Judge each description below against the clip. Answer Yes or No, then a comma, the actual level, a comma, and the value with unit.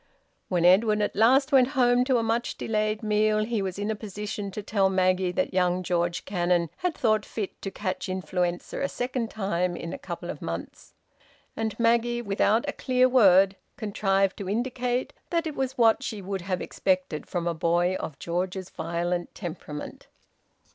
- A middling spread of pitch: Yes, average, 4.3 semitones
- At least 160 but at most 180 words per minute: Yes, average, 175 wpm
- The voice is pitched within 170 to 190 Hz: No, high, 200 Hz